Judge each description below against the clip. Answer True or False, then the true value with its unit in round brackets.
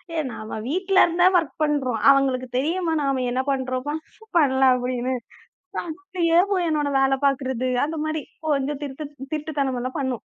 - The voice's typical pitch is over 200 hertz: True (280 Hz)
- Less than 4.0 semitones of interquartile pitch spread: True (3.4 semitones)